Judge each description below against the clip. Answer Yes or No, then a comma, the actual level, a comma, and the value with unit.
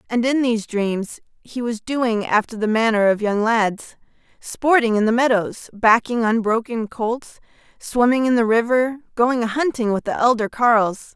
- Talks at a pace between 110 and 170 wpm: Yes, average, 165 wpm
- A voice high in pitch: Yes, high, 230 Hz